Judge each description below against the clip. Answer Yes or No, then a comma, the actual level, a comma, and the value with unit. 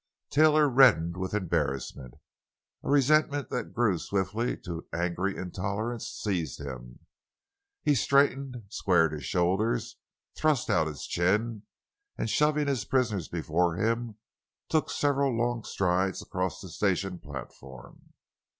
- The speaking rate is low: Yes, slow, 125 wpm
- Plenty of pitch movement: Yes, wide, 6.4 semitones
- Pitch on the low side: Yes, low, 100 Hz